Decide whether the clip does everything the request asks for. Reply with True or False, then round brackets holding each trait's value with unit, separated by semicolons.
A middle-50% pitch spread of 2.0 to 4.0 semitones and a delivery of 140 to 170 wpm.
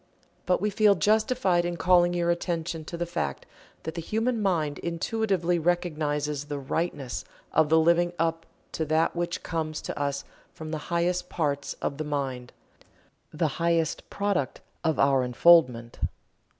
True (2.9 semitones; 150 wpm)